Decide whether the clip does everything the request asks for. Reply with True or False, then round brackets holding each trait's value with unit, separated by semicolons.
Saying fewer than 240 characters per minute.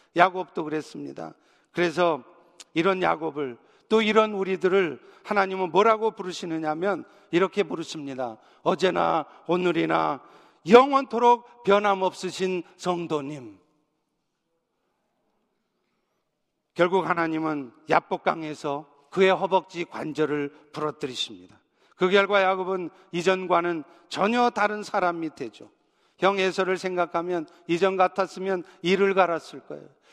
False (260 characters per minute)